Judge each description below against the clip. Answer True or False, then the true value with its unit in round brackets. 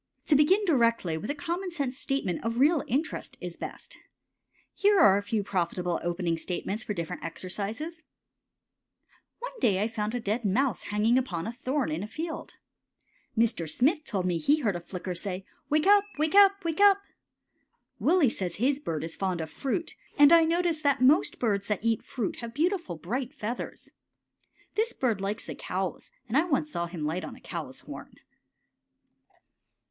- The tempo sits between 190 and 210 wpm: False (175 wpm)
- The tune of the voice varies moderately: False (8.2 semitones)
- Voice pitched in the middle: False (235 Hz)